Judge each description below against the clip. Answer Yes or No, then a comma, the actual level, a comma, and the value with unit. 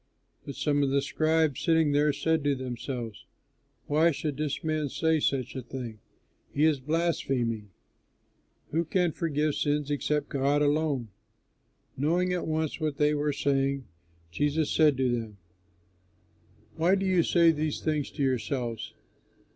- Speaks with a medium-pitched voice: Yes, medium, 145 Hz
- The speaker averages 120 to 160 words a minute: Yes, average, 145 wpm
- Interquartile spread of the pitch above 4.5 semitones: No, average, 2.8 semitones